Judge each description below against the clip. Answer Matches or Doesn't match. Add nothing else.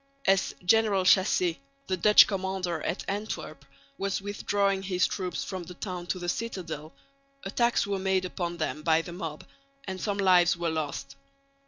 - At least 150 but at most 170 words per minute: Matches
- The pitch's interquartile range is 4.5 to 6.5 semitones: Doesn't match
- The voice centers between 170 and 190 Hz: Matches